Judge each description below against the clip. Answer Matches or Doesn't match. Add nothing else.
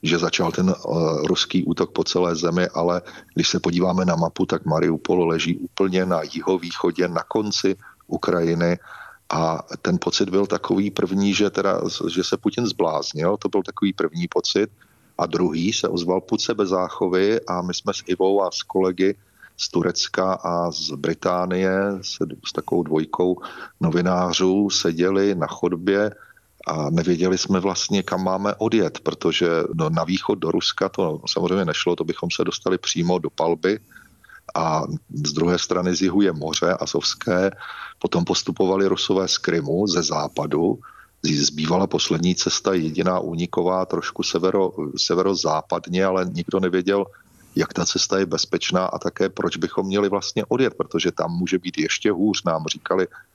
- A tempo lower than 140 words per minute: Doesn't match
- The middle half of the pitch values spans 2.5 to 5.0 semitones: Doesn't match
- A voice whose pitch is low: Matches